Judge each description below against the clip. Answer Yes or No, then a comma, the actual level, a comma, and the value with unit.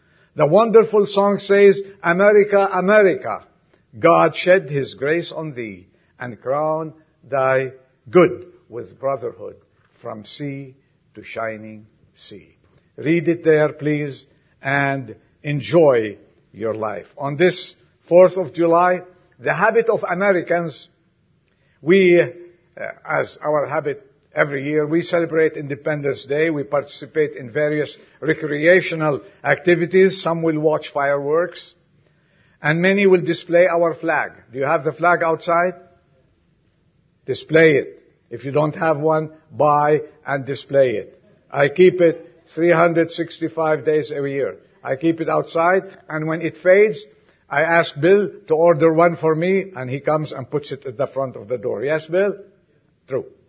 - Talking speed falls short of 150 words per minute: Yes, slow, 135 wpm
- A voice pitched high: No, medium, 160 Hz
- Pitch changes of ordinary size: Yes, average, 3.6 semitones